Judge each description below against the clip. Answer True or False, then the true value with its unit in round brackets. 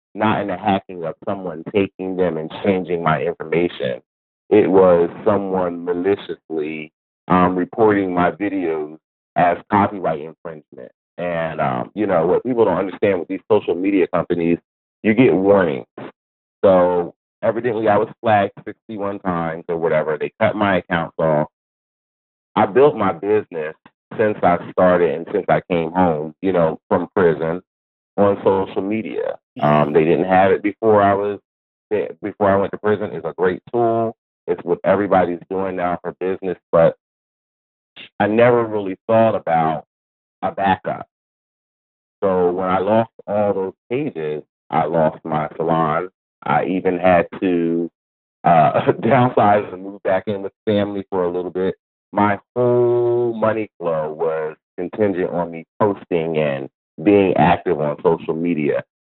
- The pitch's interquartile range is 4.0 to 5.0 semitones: False (3.5 semitones)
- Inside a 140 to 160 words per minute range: True (150 wpm)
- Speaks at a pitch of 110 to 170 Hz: False (95 Hz)